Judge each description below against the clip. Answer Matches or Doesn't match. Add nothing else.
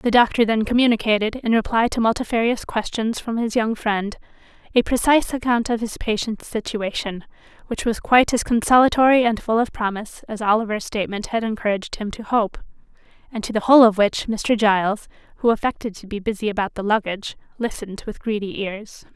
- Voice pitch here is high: Matches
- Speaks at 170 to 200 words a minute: Matches